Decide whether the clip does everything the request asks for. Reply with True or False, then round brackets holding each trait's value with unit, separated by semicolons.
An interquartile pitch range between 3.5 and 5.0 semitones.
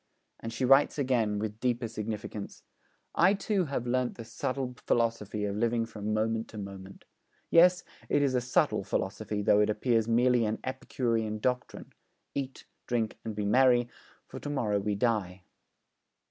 False (3.1 semitones)